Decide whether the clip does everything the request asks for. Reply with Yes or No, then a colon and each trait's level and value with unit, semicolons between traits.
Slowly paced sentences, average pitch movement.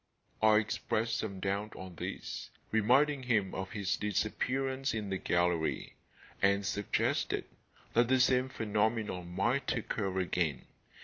Yes: slow, 125 wpm; average, 3.8 semitones